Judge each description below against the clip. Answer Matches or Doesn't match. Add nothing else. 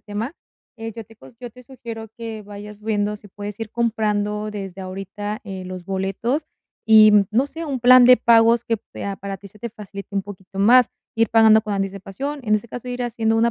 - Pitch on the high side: Matches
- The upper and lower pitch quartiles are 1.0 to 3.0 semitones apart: Matches